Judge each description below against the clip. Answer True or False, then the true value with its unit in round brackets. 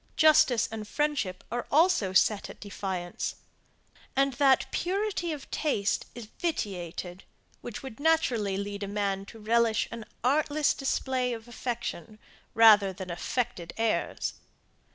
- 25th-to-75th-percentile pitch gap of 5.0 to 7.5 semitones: True (5.5 semitones)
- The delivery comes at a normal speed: False (130 wpm)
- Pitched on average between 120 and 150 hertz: False (230 Hz)